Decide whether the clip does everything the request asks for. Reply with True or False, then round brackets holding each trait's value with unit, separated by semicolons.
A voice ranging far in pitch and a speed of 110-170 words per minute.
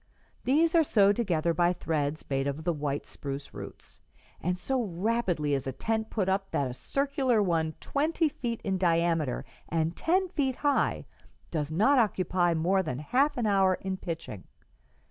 True (7.0 semitones; 165 wpm)